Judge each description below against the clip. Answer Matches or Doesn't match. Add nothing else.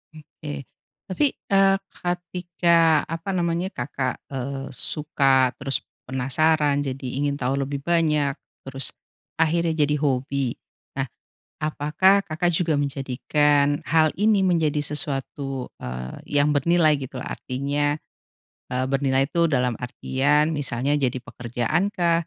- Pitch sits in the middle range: Matches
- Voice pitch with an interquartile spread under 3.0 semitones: Doesn't match